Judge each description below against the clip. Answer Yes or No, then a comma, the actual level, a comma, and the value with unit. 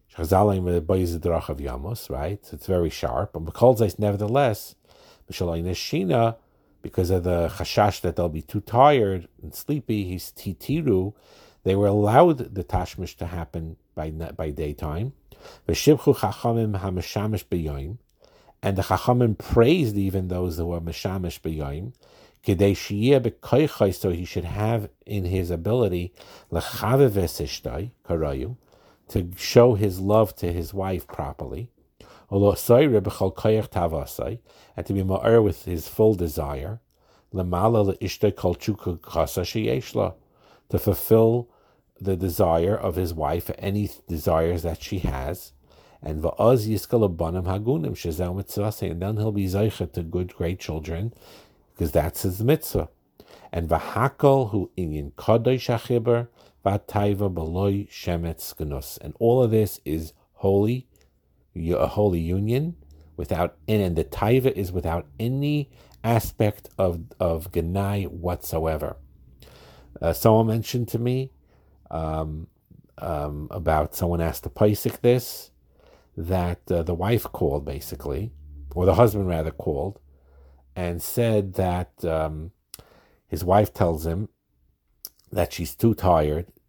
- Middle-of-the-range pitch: No, very low, 95 Hz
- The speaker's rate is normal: No, slow, 110 wpm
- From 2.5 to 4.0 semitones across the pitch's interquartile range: No, average, 4.6 semitones